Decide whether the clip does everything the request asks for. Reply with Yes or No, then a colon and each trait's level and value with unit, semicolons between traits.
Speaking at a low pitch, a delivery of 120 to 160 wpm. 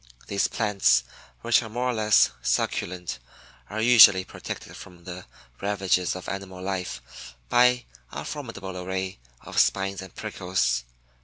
Yes: very low, 95 Hz; slow, 135 wpm